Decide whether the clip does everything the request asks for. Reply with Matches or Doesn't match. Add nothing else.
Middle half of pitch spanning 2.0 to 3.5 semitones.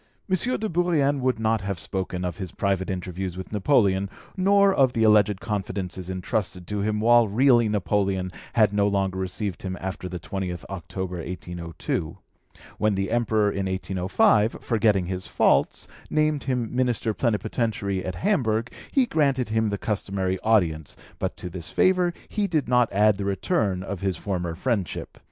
Doesn't match